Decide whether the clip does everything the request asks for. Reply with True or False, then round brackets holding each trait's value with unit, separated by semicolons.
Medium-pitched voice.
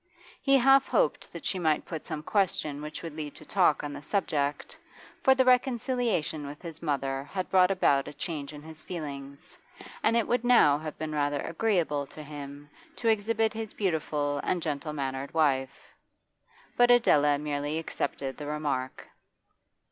True (155 Hz)